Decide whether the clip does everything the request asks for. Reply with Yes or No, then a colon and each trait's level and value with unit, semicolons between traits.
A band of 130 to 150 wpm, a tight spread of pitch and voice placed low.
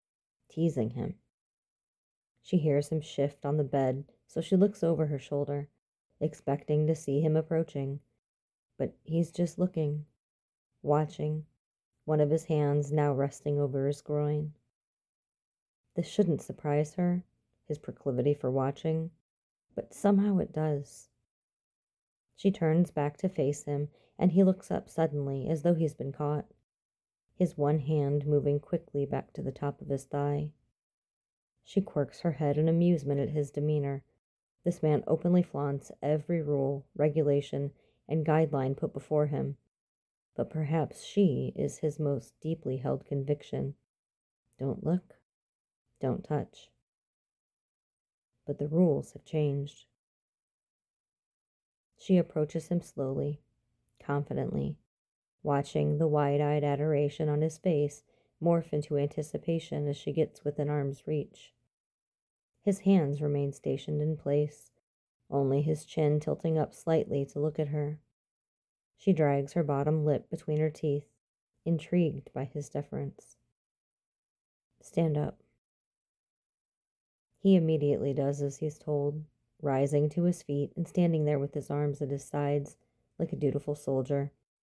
No: slow, 135 wpm; narrow, 2.0 semitones; medium, 150 Hz